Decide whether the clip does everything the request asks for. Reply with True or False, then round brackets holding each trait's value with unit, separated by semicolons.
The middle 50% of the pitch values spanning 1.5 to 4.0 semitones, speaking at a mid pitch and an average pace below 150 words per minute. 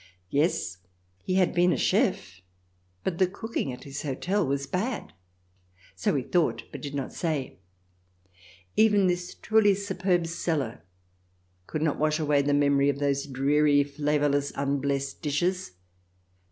False (4.4 semitones; 145 Hz; 140 wpm)